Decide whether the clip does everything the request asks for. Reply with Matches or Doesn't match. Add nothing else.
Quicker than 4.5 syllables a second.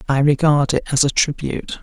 Matches